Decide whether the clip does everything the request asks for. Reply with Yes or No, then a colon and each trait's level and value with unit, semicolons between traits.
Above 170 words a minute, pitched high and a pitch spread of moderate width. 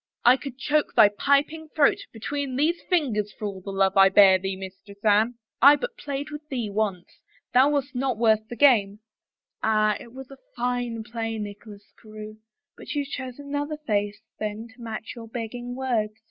Yes: average, 190 wpm; high, 230 Hz; average, 4.6 semitones